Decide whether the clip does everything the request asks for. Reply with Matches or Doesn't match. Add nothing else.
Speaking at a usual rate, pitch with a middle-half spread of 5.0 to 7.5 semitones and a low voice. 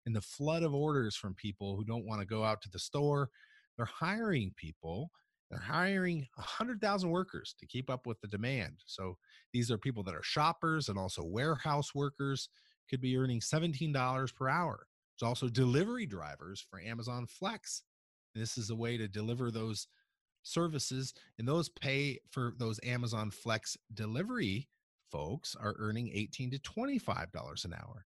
Matches